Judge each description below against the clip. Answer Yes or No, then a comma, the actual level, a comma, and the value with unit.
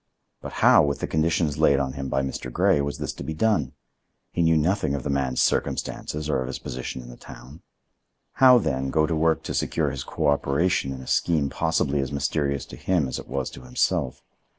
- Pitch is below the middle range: Yes, very low, 70 Hz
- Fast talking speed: Yes, fast, 215 wpm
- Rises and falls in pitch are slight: No, average, 3.0 semitones